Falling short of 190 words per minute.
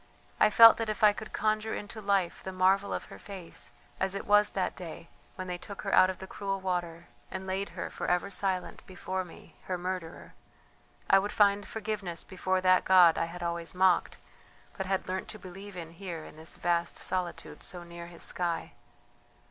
No: average, 195 wpm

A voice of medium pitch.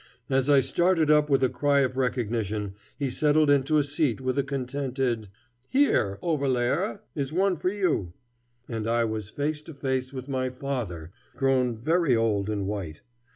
No: low, 130 Hz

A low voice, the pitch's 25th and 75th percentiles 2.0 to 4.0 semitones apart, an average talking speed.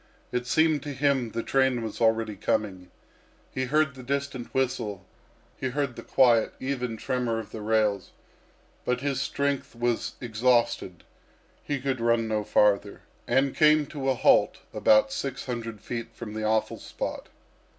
Yes: low, 120 Hz; average, 3.4 semitones; average, 155 wpm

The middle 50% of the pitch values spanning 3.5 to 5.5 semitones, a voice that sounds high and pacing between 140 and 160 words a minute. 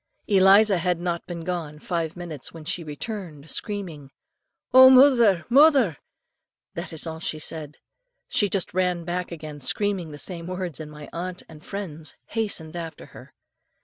No: average, 3.8 semitones; medium, 175 Hz; average, 155 wpm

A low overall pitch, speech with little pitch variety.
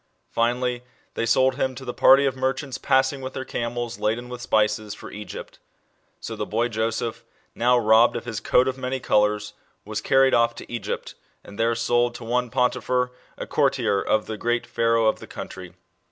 Yes: low, 120 Hz; narrow, 2.3 semitones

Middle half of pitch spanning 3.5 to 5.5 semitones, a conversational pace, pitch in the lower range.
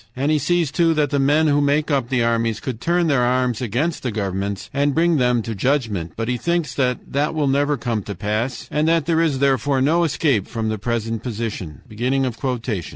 No: average, 4.7 semitones; fast, 210 wpm; low, 130 Hz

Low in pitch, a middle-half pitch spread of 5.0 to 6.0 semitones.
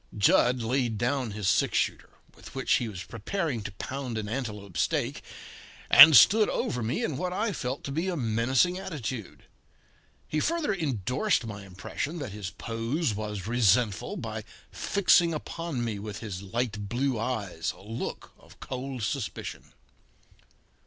Yes: low, 120 Hz; wide, 5.5 semitones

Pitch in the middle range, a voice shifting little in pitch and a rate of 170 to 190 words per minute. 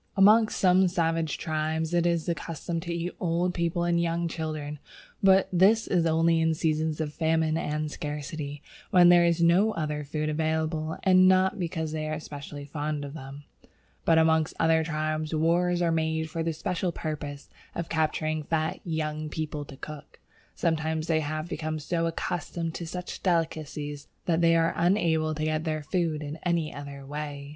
Yes: medium, 160 Hz; narrow, 1.8 semitones; average, 175 wpm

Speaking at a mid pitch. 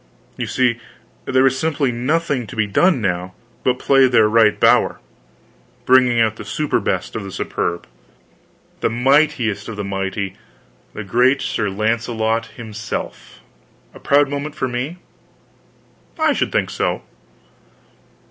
No: low, 120 Hz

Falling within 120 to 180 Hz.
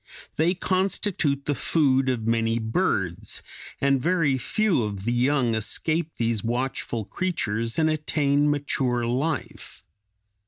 Yes: low, 135 Hz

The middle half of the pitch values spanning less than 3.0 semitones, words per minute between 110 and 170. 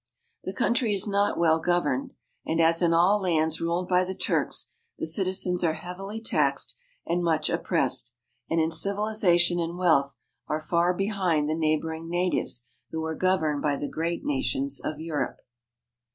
Yes: narrow, 2.5 semitones; average, 160 wpm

